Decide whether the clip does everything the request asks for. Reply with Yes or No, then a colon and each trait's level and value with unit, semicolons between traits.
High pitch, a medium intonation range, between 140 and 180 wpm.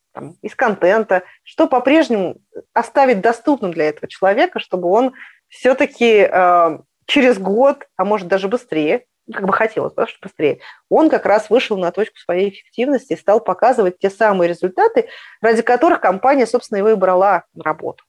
No: high, 220 Hz; wide, 5.7 semitones; average, 155 wpm